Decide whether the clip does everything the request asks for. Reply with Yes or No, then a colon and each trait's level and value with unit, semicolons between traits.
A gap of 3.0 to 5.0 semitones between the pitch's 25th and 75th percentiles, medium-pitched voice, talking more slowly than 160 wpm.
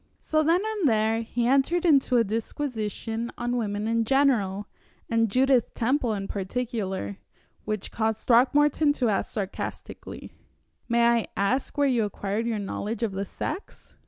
No: average, 4.0 semitones; high, 230 Hz; average, 150 wpm